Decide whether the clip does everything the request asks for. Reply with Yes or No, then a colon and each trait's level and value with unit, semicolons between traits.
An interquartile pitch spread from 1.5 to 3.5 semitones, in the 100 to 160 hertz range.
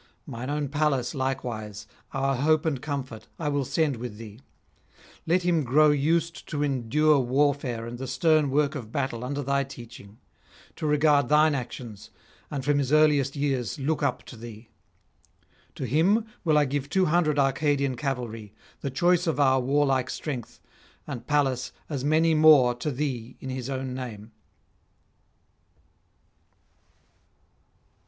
Yes: average, 3.2 semitones; medium, 140 Hz